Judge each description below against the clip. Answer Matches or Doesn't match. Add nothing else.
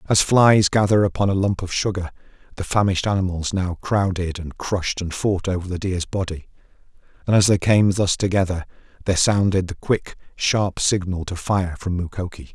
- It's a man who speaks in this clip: Matches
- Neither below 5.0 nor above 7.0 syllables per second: Matches